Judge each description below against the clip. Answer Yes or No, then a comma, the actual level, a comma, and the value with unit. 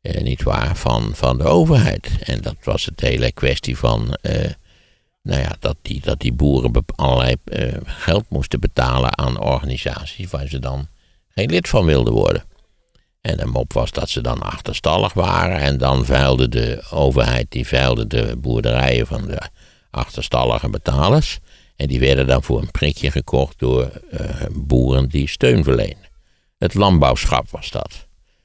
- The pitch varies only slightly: Yes, narrow, 2.3 semitones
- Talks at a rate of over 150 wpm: Yes, average, 160 wpm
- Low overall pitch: Yes, very low, 65 Hz